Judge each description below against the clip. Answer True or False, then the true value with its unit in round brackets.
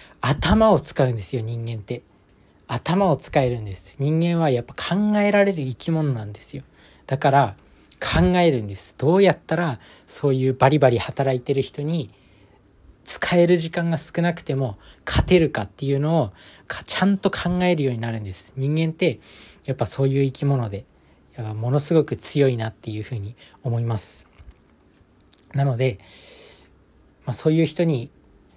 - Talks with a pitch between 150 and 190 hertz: False (130 Hz)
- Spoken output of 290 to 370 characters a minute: True (315 characters per minute)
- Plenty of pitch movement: True (6.9 semitones)